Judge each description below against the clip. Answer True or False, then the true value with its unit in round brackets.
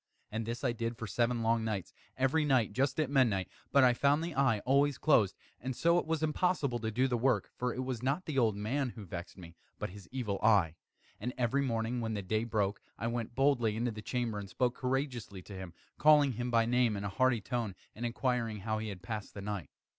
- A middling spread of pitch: True (3.6 semitones)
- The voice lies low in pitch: True (120 Hz)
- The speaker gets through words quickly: True (230 wpm)